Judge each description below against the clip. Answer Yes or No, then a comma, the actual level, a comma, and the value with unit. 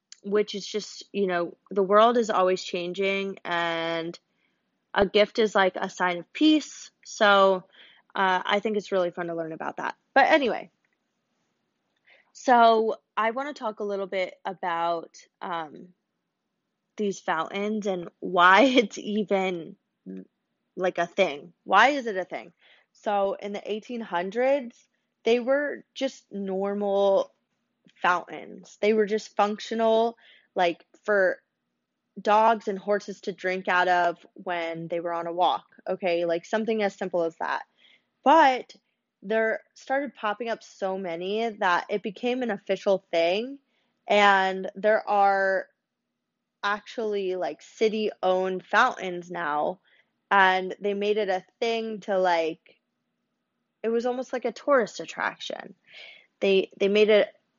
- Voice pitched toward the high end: Yes, high, 200 Hz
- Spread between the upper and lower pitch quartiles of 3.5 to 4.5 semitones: No, average, 3.1 semitones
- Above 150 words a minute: No, slow, 135 wpm